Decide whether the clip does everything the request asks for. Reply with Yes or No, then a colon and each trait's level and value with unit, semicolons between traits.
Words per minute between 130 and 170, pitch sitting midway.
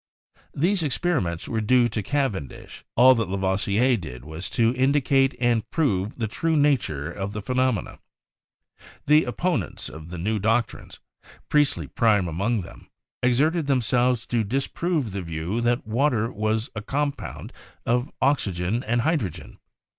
No: average, 140 wpm; low, 115 Hz